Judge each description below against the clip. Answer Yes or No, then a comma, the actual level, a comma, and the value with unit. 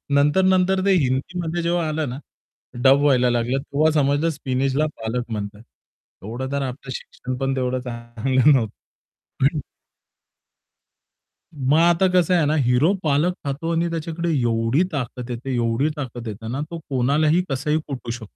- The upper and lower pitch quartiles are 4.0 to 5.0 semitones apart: Yes, average, 4.3 semitones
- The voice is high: No, low, 135 Hz